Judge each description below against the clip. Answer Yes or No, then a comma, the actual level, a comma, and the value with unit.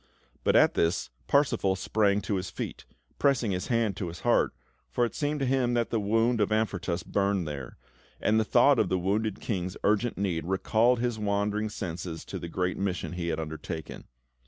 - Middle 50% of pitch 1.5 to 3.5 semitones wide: No, average, 4.0 semitones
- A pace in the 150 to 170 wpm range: No, average, 190 wpm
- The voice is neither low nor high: No, low, 100 Hz